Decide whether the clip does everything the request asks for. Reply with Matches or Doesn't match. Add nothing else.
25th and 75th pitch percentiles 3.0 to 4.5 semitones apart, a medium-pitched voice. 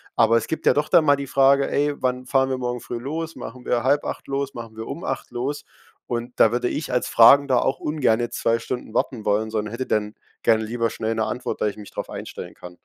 Doesn't match